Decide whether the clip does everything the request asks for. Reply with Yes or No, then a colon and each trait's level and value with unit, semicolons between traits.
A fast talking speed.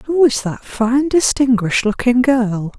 No: average, 150 wpm